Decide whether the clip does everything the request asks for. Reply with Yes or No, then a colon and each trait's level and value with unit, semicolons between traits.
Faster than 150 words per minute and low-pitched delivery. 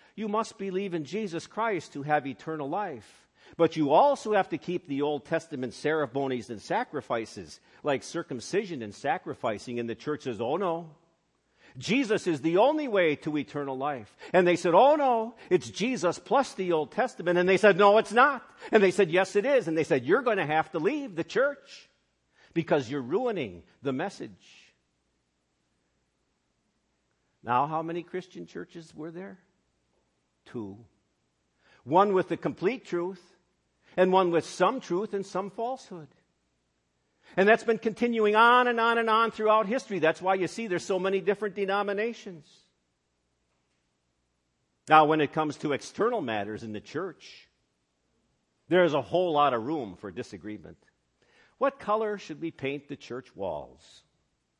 No: average, 160 wpm; medium, 165 Hz